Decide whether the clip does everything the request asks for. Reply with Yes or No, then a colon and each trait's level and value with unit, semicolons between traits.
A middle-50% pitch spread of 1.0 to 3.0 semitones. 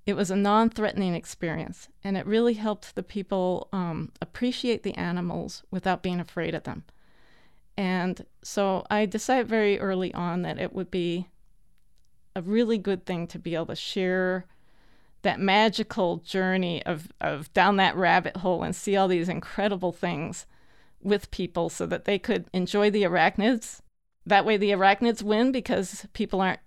Yes: average, 2.7 semitones